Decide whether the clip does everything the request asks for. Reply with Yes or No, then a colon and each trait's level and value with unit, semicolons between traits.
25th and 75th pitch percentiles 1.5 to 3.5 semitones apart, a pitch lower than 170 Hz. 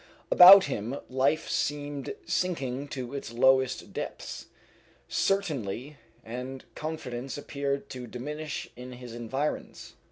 Yes: average, 2.9 semitones; low, 135 Hz